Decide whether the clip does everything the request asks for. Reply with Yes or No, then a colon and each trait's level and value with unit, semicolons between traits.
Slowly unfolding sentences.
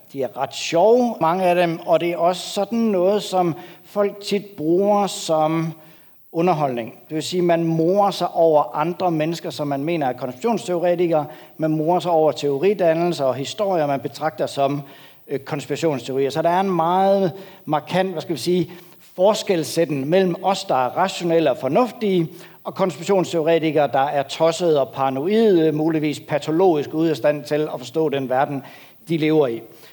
No: average, 165 wpm